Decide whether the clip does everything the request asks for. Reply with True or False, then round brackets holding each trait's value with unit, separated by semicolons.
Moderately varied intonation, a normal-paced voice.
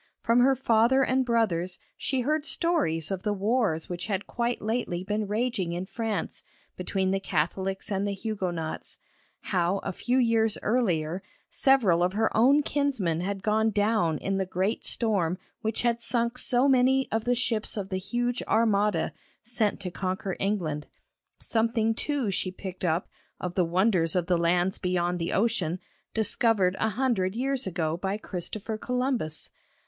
True (4.4 semitones; 160 wpm)